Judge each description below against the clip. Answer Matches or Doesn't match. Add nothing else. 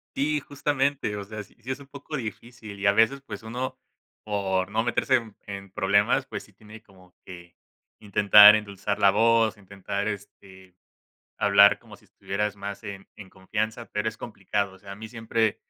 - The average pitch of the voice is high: Doesn't match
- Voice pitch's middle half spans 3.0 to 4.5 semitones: Doesn't match